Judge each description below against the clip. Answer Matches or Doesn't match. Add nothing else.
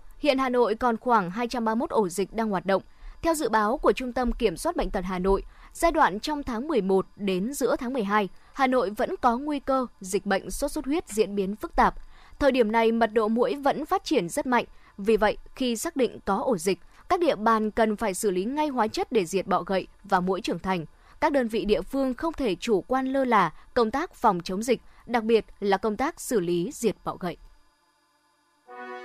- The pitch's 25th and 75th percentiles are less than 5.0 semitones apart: Doesn't match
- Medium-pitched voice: Doesn't match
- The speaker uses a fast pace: Doesn't match